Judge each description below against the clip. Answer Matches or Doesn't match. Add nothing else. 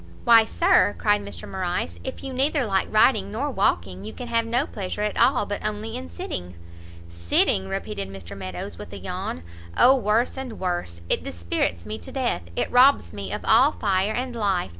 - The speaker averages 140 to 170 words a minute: Doesn't match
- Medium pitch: Doesn't match